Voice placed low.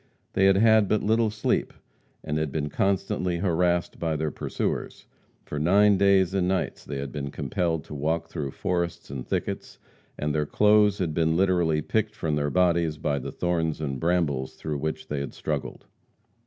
Yes: very low, 85 Hz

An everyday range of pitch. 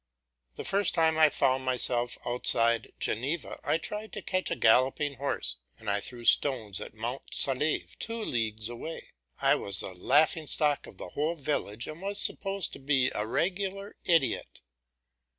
No: wide, 5.8 semitones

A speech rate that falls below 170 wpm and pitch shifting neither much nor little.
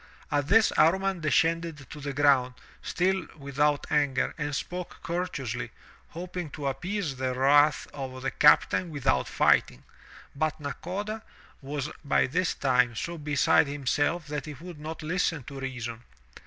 Yes: average, 145 wpm; average, 3.8 semitones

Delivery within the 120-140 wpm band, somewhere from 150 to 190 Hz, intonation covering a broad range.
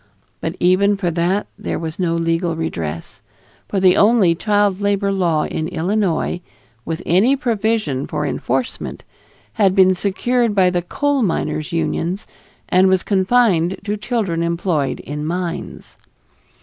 No: slow, 135 wpm; medium, 185 Hz; average, 3.6 semitones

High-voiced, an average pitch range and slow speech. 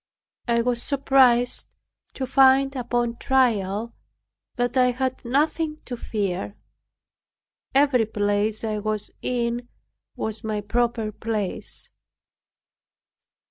Yes: high, 240 Hz; average, 3.3 semitones; slow, 100 wpm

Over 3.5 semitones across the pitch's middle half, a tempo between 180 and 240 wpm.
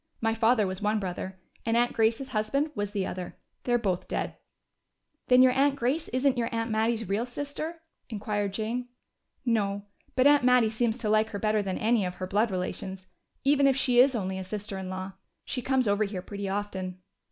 Yes: average, 3.9 semitones; average, 200 wpm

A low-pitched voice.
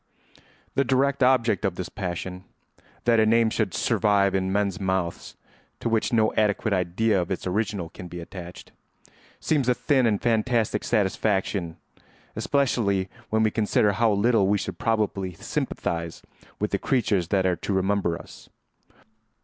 Yes: low, 100 Hz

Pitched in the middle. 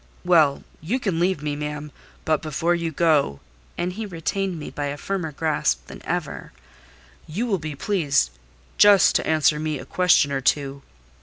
Yes: medium, 155 Hz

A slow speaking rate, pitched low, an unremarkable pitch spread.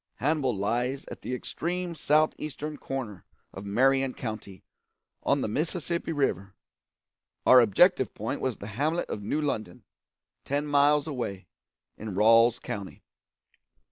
No: slow, 130 wpm; low, 130 Hz; wide, 5.9 semitones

